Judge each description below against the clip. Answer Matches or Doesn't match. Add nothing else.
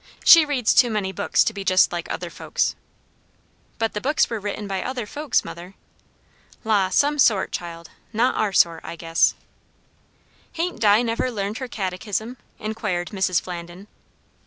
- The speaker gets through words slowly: Doesn't match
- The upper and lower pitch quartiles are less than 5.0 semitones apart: Matches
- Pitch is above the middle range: Matches